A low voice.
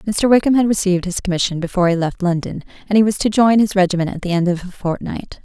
No: high, 190 Hz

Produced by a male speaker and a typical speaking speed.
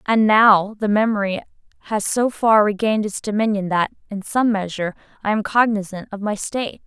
No: female; average, 175 wpm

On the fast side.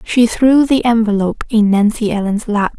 No: average, 170 wpm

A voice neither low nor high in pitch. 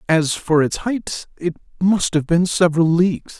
Yes: medium, 170 Hz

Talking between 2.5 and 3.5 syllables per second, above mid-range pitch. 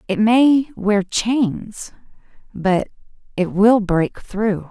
Yes: 2.7 syllables/s; high, 210 Hz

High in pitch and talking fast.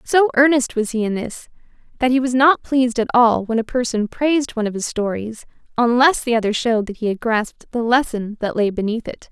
Yes: high, 235 Hz; fast, 225 wpm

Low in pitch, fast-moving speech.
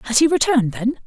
No: very high, 255 Hz; fast, 225 wpm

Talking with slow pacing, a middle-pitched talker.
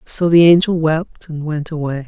No: average, 200 wpm; medium, 160 Hz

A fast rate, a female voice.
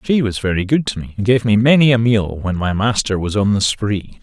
No: fast, 270 wpm; male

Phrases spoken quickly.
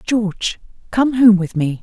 No: average, 165 wpm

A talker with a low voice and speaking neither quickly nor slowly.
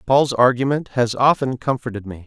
Yes: low, 125 Hz; average, 160 wpm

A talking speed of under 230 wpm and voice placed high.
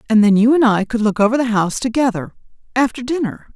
Yes: average, 200 wpm; high, 230 Hz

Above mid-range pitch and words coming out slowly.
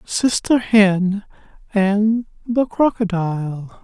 Yes: high, 205 Hz; slow, 80 wpm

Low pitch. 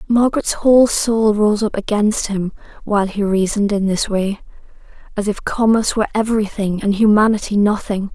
No: high, 210 Hz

